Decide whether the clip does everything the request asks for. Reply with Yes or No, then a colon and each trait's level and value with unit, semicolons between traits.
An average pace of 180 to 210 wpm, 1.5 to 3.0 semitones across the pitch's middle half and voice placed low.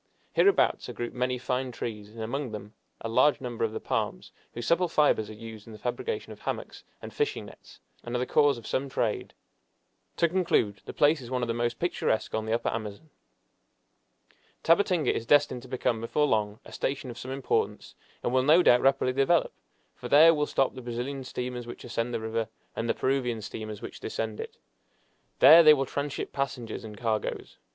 No: average, 200 wpm; average, 3.9 semitones; low, 125 Hz